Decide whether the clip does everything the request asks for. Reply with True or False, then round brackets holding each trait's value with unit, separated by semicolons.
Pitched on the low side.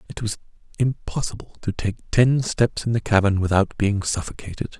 True (105 Hz)